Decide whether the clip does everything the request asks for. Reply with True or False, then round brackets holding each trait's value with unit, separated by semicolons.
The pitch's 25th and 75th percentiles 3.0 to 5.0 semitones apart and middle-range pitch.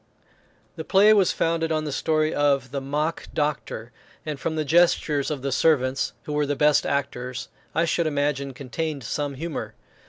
False (2.5 semitones; 150 Hz)